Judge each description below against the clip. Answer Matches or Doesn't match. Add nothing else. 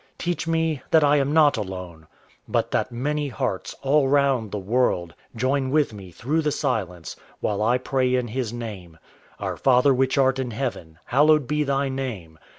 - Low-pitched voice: Matches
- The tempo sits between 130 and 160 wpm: Doesn't match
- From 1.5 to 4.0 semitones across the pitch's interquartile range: Doesn't match